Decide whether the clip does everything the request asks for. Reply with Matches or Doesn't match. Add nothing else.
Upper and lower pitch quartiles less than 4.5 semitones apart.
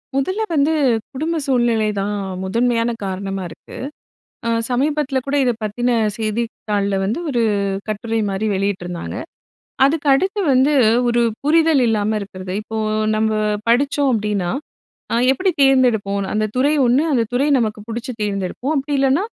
Doesn't match